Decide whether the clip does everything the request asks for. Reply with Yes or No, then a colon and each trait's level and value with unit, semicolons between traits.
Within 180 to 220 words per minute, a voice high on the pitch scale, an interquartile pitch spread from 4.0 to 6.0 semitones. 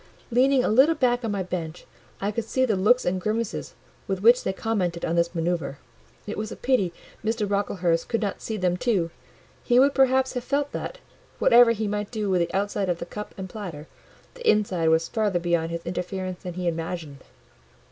Yes: average, 200 wpm; high, 200 Hz; average, 4.8 semitones